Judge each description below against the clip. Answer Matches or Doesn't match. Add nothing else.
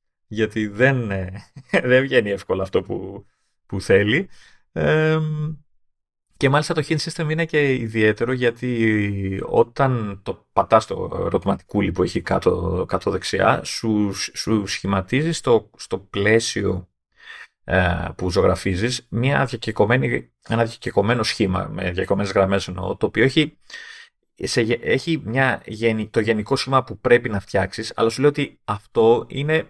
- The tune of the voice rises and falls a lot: Matches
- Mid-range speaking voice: Doesn't match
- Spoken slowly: Doesn't match